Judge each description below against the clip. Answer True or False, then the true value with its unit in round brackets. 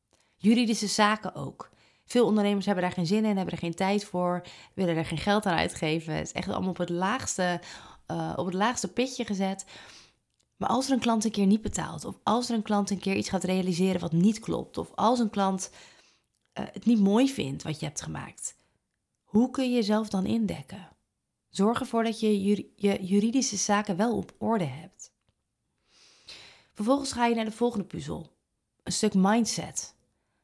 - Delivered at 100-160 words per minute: False (190 wpm)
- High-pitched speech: True (200 Hz)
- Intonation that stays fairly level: False (3.8 semitones)